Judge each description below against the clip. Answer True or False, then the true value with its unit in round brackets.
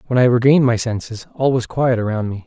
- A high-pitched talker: False (120 Hz)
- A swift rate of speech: True (245 wpm)